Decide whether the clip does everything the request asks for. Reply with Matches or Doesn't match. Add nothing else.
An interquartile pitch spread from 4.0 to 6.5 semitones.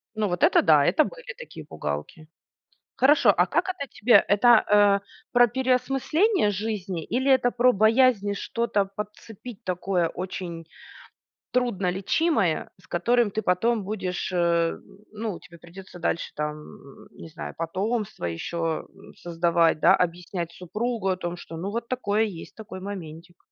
Matches